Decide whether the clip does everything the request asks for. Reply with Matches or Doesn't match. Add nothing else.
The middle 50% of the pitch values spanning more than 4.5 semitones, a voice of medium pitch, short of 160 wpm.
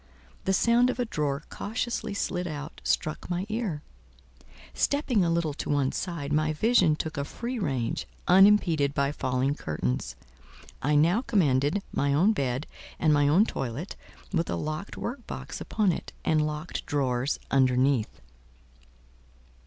Matches